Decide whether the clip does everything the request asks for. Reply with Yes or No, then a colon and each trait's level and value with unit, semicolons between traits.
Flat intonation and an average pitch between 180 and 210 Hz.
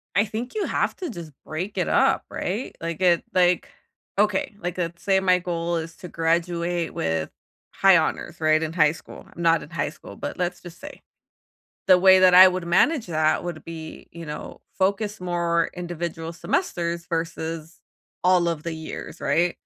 No: narrow, 2.0 semitones; medium, 170 Hz